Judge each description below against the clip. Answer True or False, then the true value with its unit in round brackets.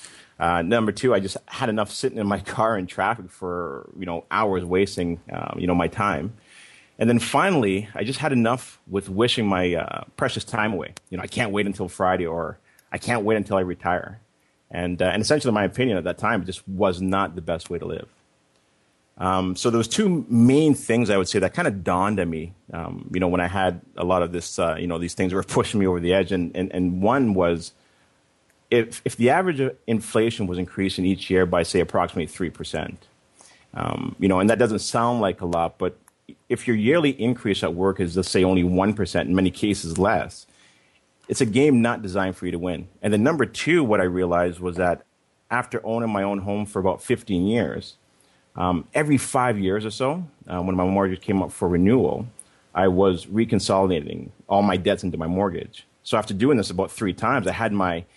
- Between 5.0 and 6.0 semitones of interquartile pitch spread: False (4.1 semitones)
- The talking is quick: True (220 wpm)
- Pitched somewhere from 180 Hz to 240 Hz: False (95 Hz)